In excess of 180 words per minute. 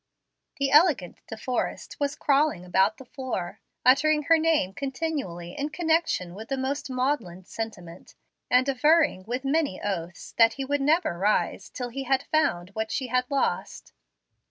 No: average, 155 wpm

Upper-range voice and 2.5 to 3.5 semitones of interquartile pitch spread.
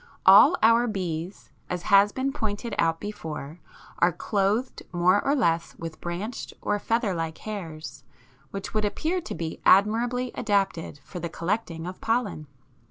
No: high, 200 Hz; average, 5.1 semitones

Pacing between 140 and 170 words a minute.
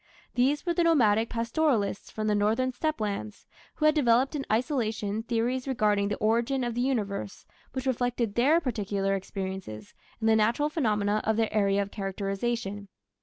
Yes: average, 165 wpm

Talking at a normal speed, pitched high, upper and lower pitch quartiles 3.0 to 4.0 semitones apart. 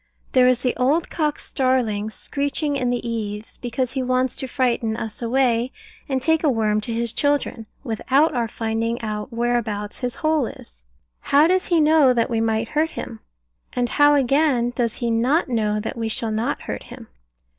Yes: average, 185 wpm; high, 245 Hz; average, 3.5 semitones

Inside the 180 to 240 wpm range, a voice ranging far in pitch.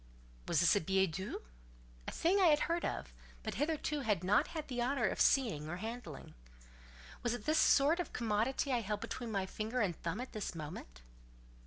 Yes: average, 195 wpm; wide, 6.4 semitones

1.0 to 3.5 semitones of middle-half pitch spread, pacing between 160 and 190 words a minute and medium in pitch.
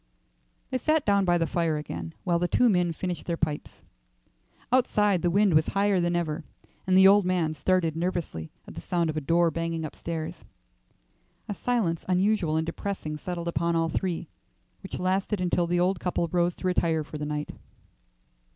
Yes: narrow, 2.5 semitones; average, 180 wpm; medium, 175 Hz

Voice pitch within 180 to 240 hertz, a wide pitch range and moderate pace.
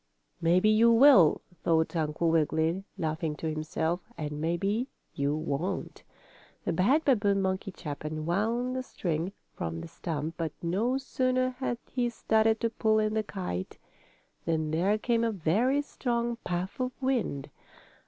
Yes: high, 190 Hz; wide, 6.5 semitones; average, 145 wpm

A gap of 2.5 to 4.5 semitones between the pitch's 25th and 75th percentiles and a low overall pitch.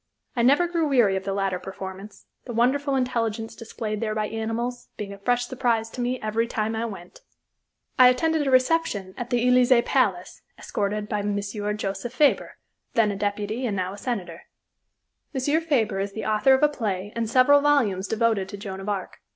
No: average, 3.9 semitones; high, 225 Hz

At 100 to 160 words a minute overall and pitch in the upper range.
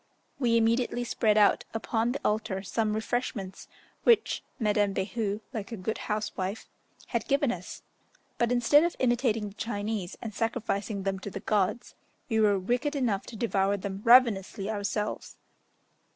Yes: average, 150 wpm; high, 215 Hz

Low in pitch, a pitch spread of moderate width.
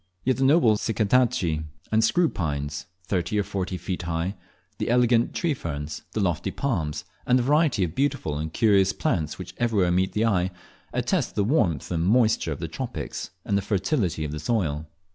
No: low, 100 Hz; wide, 6.2 semitones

